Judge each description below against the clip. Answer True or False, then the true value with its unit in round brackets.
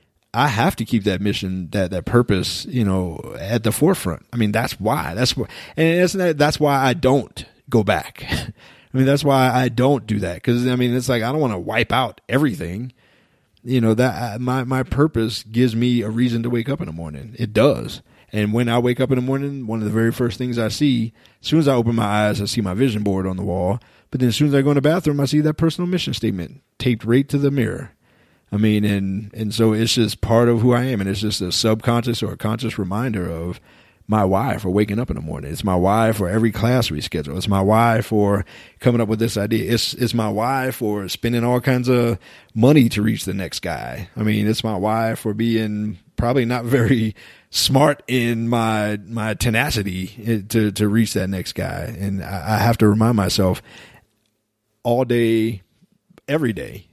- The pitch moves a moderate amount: True (3.2 semitones)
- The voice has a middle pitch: False (115 Hz)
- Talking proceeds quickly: True (220 wpm)